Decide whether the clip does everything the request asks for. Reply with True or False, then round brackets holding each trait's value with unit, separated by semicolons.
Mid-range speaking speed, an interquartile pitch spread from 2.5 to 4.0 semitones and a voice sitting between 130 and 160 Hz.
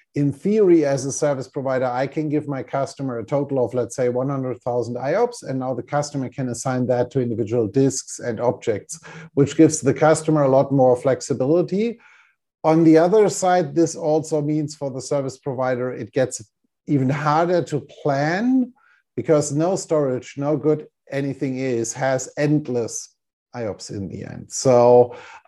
True (165 wpm; 3.3 semitones; 140 Hz)